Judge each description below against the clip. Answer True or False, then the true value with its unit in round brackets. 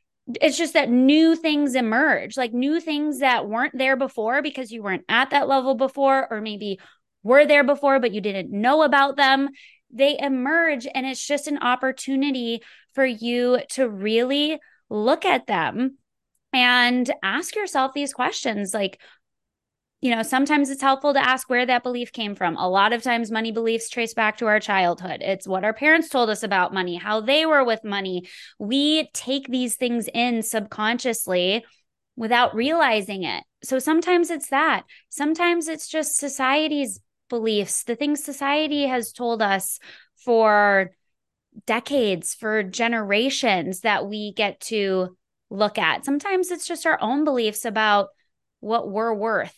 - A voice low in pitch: False (250 Hz)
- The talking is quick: False (160 wpm)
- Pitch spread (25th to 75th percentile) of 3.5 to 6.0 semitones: True (4.5 semitones)